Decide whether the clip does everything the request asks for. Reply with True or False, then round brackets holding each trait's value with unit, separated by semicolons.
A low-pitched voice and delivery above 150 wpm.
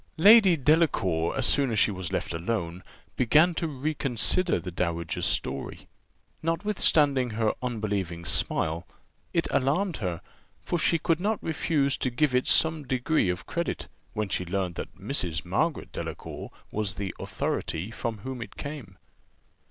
False (120 Hz; 145 wpm)